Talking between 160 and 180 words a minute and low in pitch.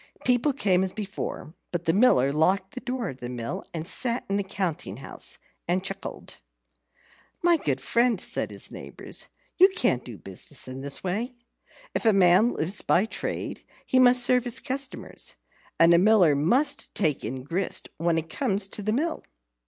No: average, 175 wpm; high, 195 Hz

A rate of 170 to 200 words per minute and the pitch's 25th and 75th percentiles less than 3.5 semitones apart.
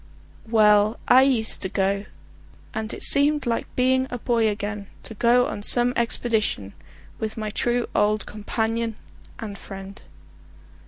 No: average, 140 wpm; narrow, 2.6 semitones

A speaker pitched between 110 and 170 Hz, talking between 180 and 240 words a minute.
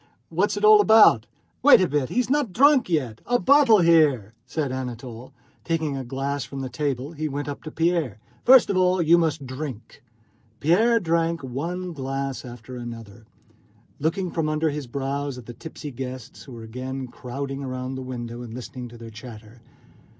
Yes: medium, 140 Hz; average, 185 wpm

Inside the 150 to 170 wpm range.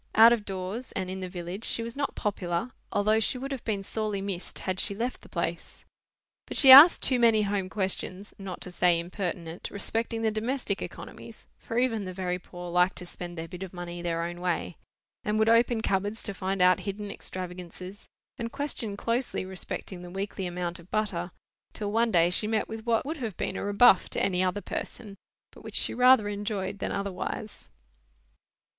No: average, 195 wpm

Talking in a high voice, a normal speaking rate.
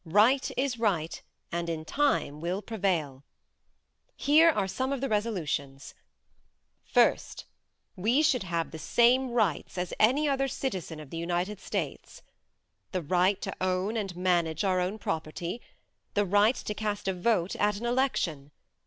Yes: high, 195 Hz; average, 150 wpm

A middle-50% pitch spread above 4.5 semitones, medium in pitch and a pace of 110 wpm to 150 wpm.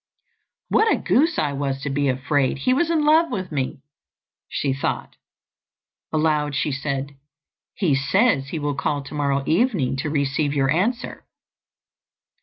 Yes: wide, 5.4 semitones; medium, 145 Hz; average, 145 wpm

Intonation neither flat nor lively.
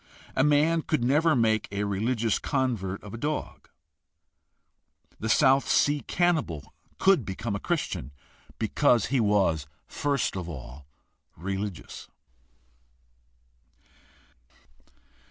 No: wide, 6.9 semitones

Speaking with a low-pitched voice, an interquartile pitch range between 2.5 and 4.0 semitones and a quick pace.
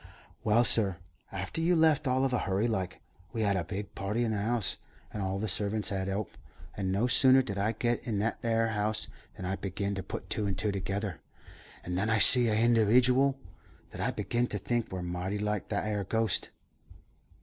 Yes: low, 105 Hz; average, 3.3 semitones; fast, 210 wpm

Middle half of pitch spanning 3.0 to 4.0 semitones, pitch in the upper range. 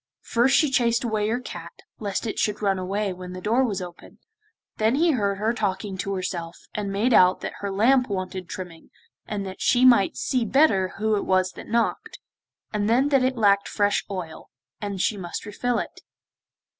Yes: average, 3.7 semitones; high, 205 Hz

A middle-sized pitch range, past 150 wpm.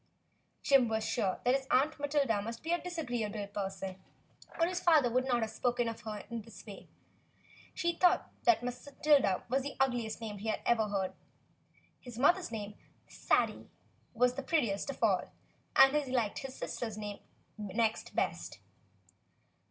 Yes: average, 4.3 semitones; average, 165 wpm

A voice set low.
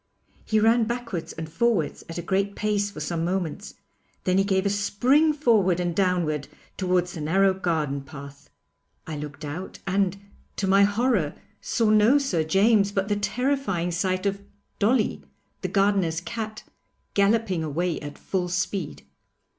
No: high, 195 Hz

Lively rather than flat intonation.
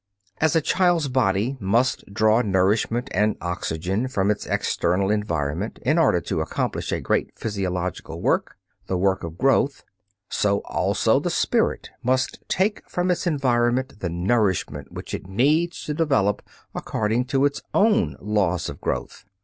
Yes: wide, 6.2 semitones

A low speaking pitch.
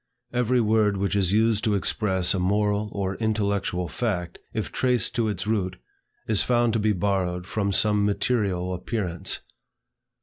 Yes: low, 105 Hz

